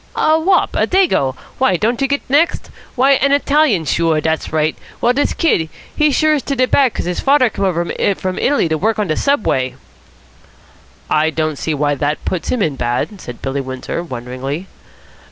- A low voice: No, medium, 185 Hz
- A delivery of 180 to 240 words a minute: Yes, average, 190 wpm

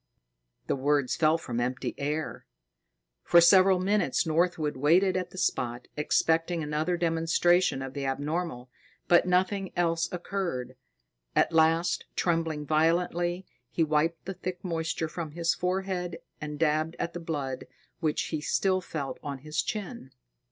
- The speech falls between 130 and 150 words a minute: Yes, average, 140 wpm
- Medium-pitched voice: Yes, medium, 165 Hz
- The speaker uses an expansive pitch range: No, average, 3.0 semitones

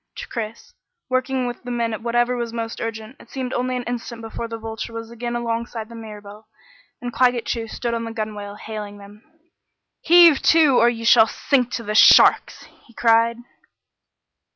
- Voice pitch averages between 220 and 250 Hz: Yes, high, 230 Hz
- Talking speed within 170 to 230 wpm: Yes, average, 180 wpm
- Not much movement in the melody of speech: Yes, narrow, 1.6 semitones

